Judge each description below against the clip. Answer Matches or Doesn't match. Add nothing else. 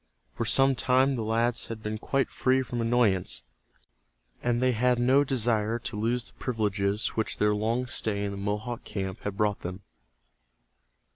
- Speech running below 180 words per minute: Matches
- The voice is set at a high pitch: Doesn't match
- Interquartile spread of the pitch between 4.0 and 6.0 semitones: Doesn't match